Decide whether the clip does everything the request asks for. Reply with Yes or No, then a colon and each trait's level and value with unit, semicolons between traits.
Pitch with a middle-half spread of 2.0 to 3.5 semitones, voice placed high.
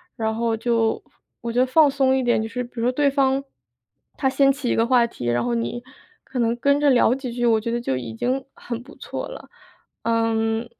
Yes: average, 2.8 semitones; high, 240 Hz